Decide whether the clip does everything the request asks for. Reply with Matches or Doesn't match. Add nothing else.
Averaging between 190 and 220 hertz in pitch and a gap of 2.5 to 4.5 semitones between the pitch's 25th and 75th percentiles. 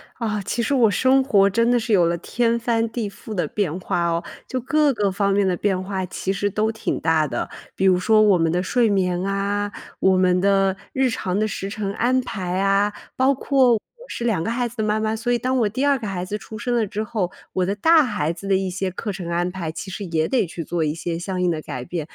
Matches